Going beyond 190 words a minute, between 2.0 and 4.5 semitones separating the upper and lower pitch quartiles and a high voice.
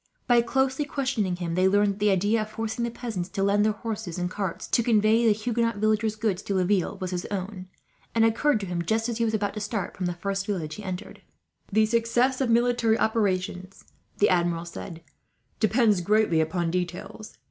Yes: average, 200 wpm; average, 3.6 semitones; high, 210 Hz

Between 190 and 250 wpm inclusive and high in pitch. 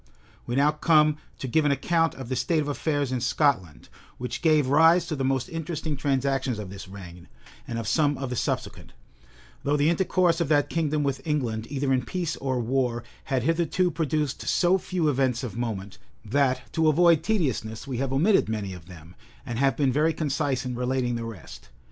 No: average, 195 wpm; low, 135 Hz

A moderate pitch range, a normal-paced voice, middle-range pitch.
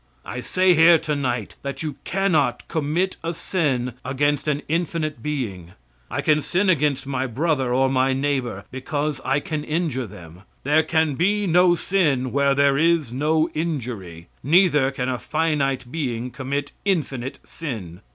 Yes: average, 3.8 semitones; average, 155 wpm; medium, 145 Hz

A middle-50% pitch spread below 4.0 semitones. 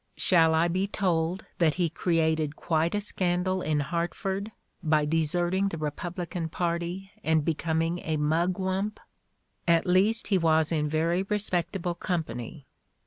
Yes: average, 2.7 semitones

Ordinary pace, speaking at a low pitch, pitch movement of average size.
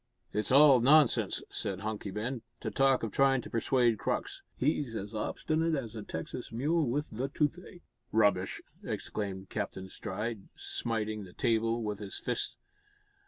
Yes: average, 150 wpm; low, 115 Hz; average, 4.5 semitones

